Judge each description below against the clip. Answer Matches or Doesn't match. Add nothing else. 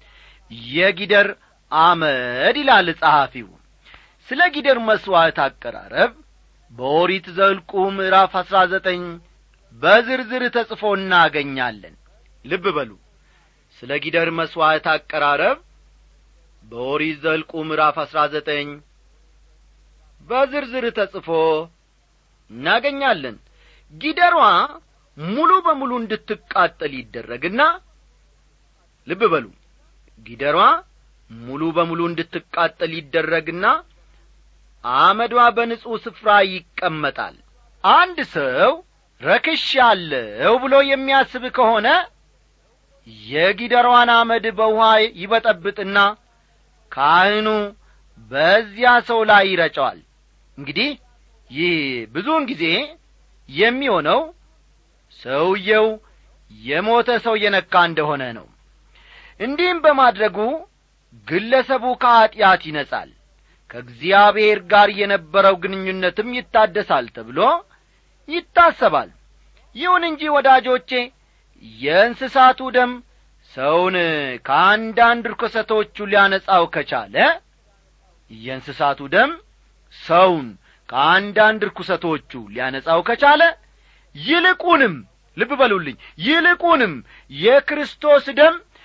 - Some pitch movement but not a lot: Doesn't match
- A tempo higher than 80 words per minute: Doesn't match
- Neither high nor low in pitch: Doesn't match